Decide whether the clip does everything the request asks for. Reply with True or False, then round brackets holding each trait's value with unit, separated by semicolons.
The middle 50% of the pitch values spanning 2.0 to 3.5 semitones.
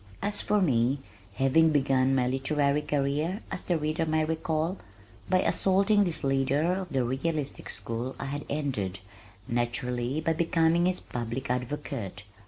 False (4.1 semitones)